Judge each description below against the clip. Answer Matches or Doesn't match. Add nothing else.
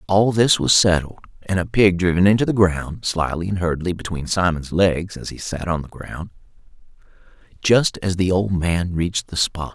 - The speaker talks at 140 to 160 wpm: Doesn't match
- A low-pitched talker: Matches